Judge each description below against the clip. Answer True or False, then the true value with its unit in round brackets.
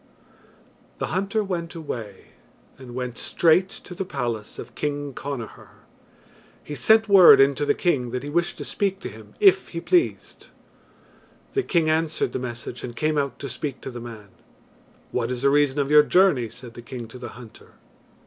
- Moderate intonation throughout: False (5.8 semitones)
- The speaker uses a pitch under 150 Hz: True (140 Hz)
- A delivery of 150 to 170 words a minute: False (185 wpm)